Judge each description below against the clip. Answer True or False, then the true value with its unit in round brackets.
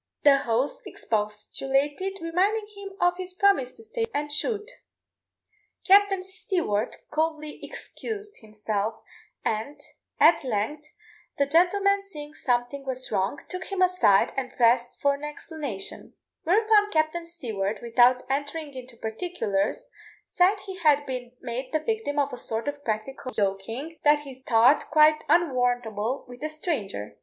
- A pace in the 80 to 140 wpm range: True (135 wpm)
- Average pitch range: False (6.6 semitones)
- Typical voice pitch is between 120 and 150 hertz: False (290 Hz)